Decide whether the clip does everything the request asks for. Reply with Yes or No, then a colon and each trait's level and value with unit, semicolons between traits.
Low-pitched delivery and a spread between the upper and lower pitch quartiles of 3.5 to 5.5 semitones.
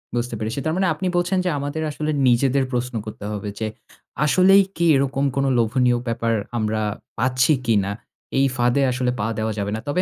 Yes: low, 125 Hz; average, 4.1 semitones